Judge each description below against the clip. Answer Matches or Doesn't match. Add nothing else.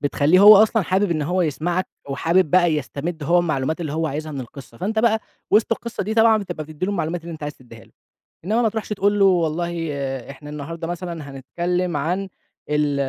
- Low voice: Doesn't match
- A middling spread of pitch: Matches